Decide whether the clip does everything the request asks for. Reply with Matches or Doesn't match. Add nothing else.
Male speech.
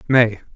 Matches